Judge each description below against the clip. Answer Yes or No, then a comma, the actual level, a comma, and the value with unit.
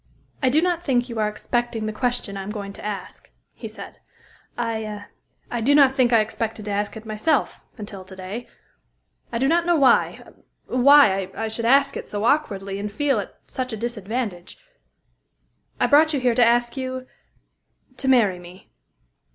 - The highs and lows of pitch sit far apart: No, average, 4.0 semitones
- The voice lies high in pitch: Yes, high, 230 Hz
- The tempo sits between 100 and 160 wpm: No, average, 175 wpm